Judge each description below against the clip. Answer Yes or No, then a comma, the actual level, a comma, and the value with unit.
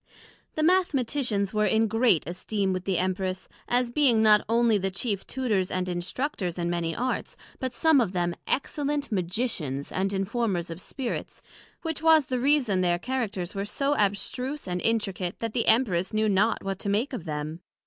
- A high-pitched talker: Yes, high, 210 Hz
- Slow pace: No, average, 175 wpm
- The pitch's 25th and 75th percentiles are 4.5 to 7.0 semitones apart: Yes, wide, 5.4 semitones